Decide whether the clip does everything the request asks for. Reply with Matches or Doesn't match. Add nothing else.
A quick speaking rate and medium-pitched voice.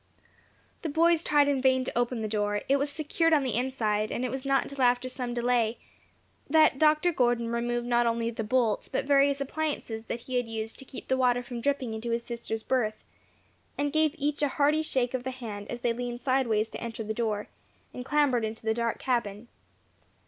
Doesn't match